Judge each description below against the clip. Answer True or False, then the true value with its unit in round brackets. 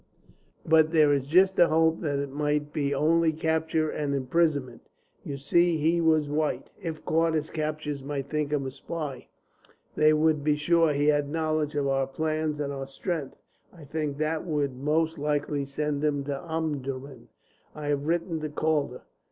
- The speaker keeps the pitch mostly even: True (2.0 semitones)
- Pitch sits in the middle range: True (150 Hz)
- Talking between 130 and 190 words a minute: True (175 wpm)